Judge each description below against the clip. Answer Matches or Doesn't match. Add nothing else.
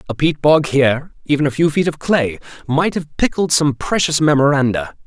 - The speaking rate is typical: Matches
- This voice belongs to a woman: Doesn't match